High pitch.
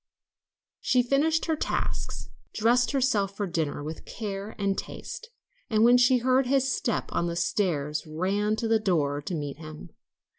Yes: high, 210 Hz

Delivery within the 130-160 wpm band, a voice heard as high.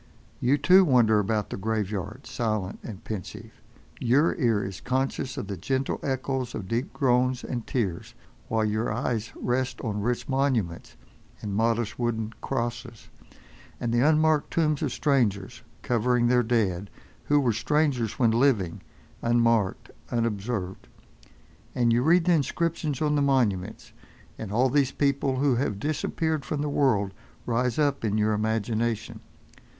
No: average, 145 wpm; low, 120 Hz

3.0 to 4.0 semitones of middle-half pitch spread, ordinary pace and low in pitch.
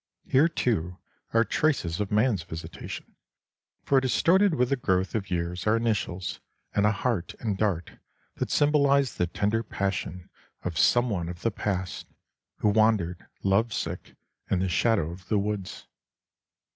No: average, 4.6 semitones; average, 150 wpm; low, 105 Hz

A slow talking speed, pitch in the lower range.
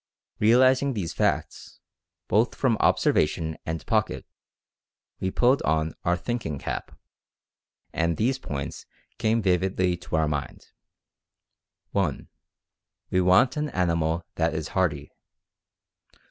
Yes: slow, 110 wpm; very low, 90 Hz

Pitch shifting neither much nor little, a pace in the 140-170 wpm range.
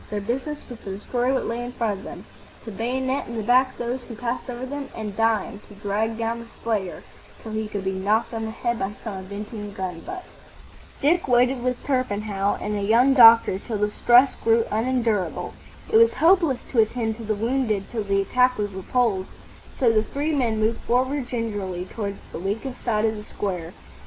No: average, 3.4 semitones; average, 200 wpm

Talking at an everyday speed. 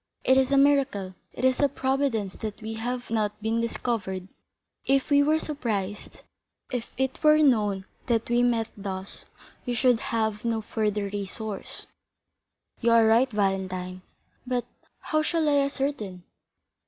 Yes: average, 145 wpm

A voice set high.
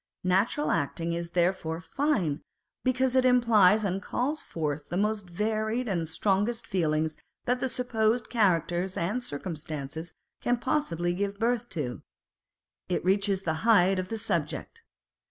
Yes: high, 195 Hz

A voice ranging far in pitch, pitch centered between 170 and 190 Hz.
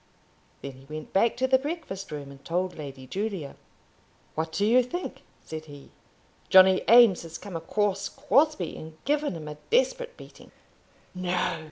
Yes: wide, 7.9 semitones; medium, 185 Hz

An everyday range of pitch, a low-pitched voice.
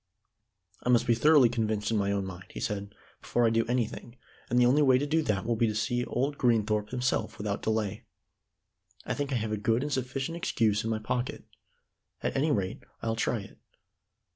Yes: average, 3.0 semitones; low, 115 Hz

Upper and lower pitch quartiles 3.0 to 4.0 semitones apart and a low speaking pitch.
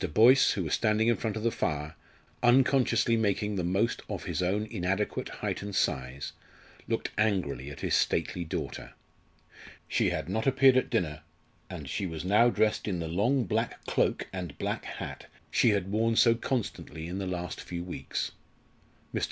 No: average, 4.8 semitones; low, 100 Hz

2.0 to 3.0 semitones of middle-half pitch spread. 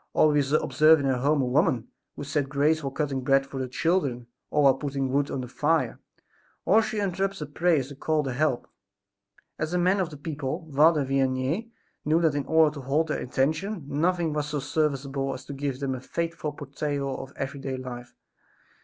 Yes: average, 2.7 semitones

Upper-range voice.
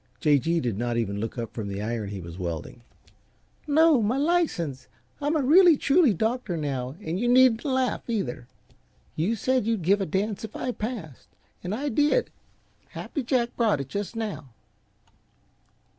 Yes: high, 205 Hz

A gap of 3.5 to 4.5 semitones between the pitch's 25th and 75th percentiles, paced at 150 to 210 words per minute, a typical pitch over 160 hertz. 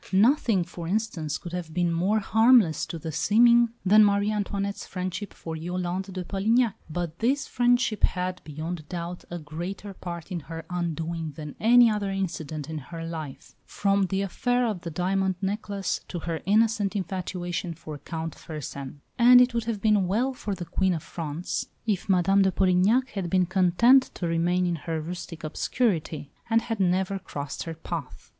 Yes: average, 3.8 semitones; average, 175 wpm; medium, 185 Hz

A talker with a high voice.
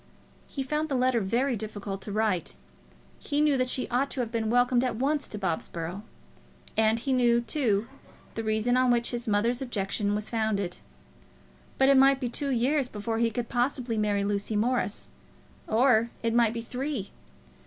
Yes: high, 235 Hz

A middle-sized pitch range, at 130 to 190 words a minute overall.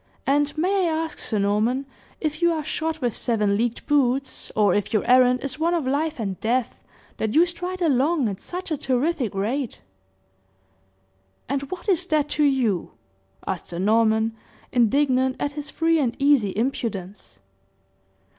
No: wide, 5.8 semitones; average, 160 wpm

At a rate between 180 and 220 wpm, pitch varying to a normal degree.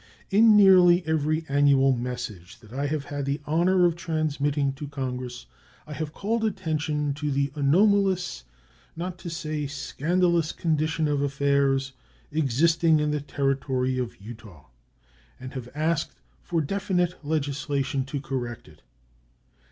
No: slow, 135 wpm; average, 3.4 semitones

